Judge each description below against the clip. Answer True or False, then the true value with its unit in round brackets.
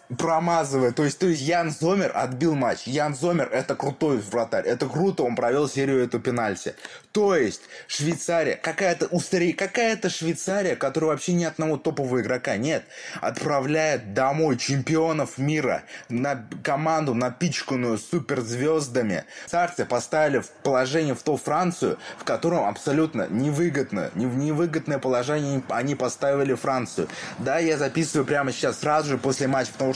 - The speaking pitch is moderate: True (145 Hz)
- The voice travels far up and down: False (3.6 semitones)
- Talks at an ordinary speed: True (140 wpm)